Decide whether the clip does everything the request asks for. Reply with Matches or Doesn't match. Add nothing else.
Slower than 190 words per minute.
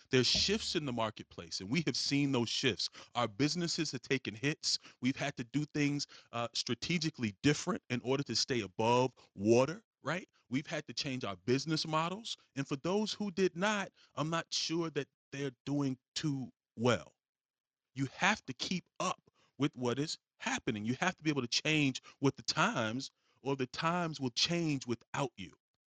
Matches